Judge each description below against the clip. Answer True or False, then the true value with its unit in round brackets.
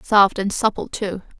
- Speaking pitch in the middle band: False (200 Hz)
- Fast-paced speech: False (170 wpm)